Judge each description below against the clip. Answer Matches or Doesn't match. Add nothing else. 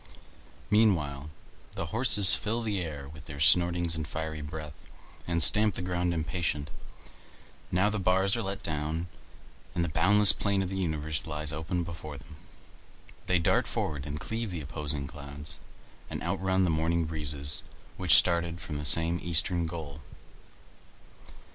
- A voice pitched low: Matches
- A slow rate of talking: Doesn't match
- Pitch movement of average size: Matches